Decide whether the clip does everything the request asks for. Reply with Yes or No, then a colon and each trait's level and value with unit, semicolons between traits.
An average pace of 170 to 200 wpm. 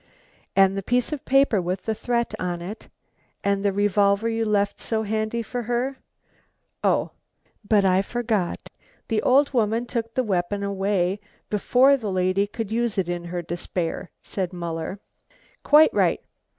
No: average, 155 wpm